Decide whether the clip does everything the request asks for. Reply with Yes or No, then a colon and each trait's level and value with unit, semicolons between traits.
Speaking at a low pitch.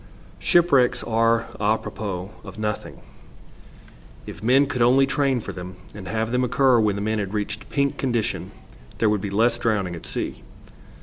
Yes: low, 115 Hz